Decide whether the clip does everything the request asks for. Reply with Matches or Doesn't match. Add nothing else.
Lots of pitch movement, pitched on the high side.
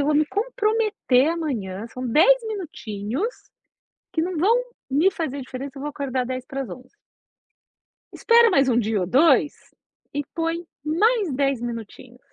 Matches